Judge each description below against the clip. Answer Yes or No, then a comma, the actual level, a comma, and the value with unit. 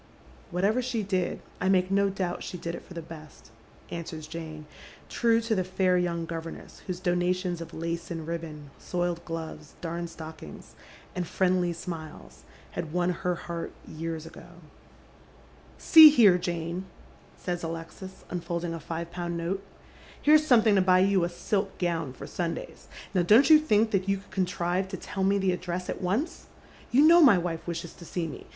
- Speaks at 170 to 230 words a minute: Yes, average, 185 wpm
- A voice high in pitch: No, medium, 175 Hz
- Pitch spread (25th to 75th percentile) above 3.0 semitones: No, narrow, 2.4 semitones